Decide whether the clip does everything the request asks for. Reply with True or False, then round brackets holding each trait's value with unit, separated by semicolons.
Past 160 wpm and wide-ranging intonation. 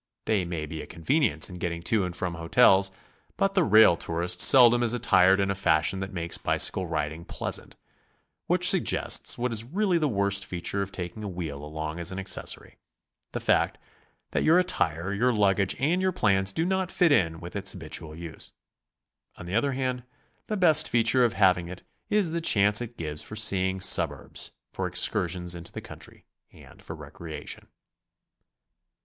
True (180 wpm; 5.9 semitones)